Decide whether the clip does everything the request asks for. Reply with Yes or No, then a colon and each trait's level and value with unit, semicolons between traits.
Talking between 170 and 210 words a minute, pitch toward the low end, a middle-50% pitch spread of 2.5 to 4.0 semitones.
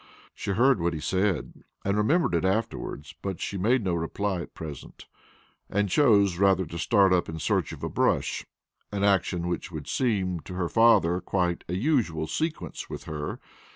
Yes: average, 180 wpm; very low, 95 Hz; average, 3.5 semitones